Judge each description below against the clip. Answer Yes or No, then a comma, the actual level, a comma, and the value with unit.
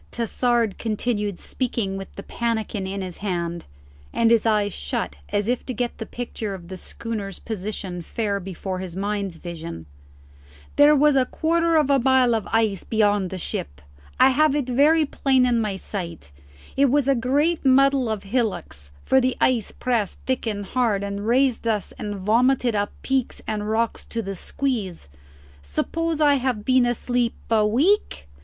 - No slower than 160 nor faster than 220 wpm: Yes, average, 170 wpm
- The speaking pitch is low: No, high, 225 Hz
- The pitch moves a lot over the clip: No, average, 4.6 semitones